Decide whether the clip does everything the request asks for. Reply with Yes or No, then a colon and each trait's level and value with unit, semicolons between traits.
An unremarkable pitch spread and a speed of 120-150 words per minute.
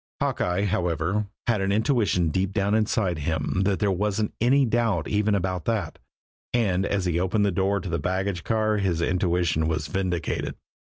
No: average, 3.3 semitones; average, 175 wpm